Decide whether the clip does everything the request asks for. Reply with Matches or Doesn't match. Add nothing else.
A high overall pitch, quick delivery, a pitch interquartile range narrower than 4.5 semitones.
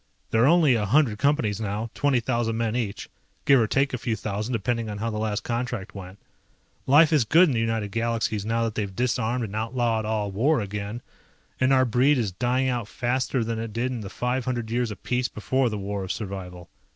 Doesn't match